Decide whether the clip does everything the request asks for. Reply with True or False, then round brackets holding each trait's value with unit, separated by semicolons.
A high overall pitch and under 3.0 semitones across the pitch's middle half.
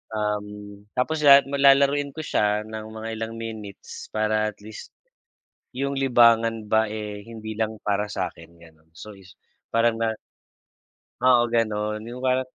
False (110 Hz; 2.5 semitones)